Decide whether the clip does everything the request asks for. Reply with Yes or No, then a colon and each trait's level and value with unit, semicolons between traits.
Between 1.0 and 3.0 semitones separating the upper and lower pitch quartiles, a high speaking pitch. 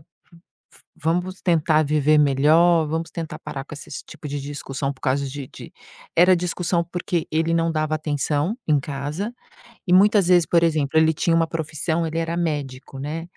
No: narrow, 2.6 semitones; medium, 160 Hz